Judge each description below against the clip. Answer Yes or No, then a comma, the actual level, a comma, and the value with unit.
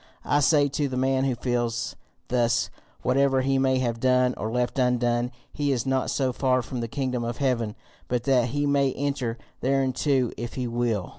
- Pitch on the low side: Yes, low, 125 Hz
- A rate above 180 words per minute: Yes, average, 190 wpm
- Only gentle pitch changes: Yes, narrow, 2.0 semitones